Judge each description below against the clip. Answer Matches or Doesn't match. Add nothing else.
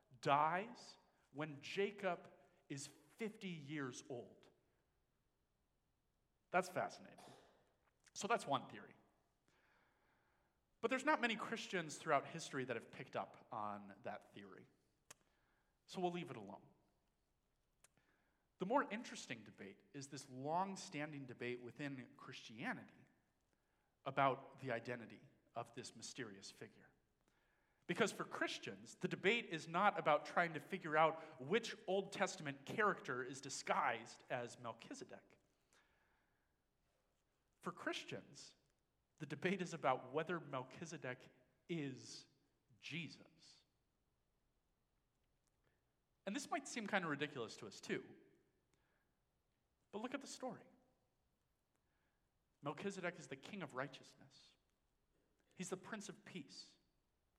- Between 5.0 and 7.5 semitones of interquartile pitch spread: Matches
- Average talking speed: Doesn't match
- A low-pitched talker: Doesn't match